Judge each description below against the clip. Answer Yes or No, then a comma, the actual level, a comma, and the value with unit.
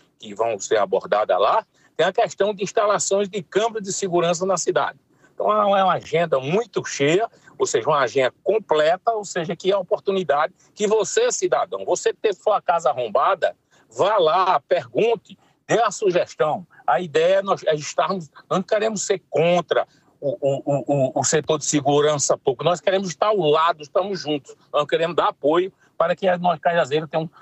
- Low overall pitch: No, medium, 185 Hz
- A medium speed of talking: Yes, average, 175 wpm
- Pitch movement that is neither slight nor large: Yes, average, 4.7 semitones